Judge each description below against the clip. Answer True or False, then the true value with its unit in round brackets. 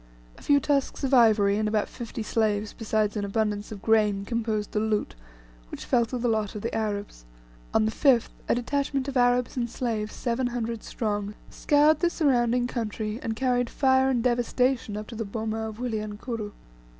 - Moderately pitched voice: False (225 Hz)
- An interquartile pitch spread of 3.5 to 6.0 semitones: False (2.7 semitones)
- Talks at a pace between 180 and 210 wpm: True (185 wpm)